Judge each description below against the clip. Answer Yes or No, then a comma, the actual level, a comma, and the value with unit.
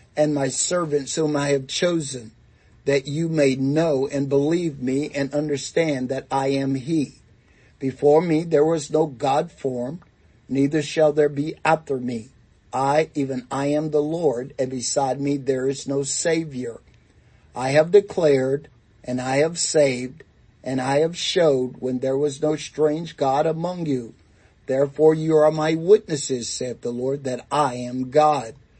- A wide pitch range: No, average, 2.8 semitones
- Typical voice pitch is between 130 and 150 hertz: Yes, medium, 140 Hz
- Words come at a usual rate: Yes, average, 160 wpm